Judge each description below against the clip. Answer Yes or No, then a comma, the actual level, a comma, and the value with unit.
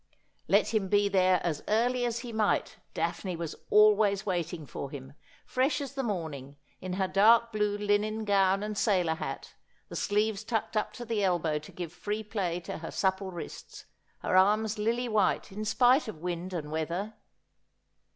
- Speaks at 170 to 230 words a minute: Yes, average, 175 wpm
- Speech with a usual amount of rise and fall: Yes, average, 3.6 semitones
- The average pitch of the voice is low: No, high, 200 Hz